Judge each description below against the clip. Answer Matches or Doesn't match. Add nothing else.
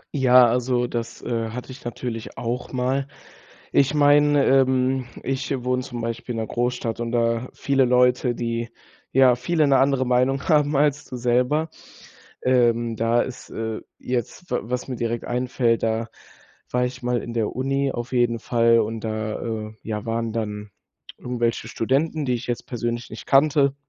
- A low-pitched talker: Matches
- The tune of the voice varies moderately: Doesn't match